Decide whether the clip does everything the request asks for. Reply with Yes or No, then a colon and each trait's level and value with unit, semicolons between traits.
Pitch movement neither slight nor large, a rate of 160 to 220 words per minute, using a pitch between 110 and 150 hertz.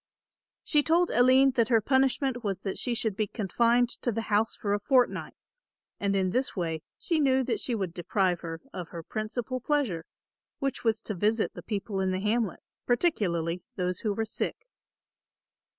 No: average, 4.8 semitones; average, 180 wpm; high, 220 Hz